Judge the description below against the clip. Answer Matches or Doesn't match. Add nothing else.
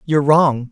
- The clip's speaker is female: Doesn't match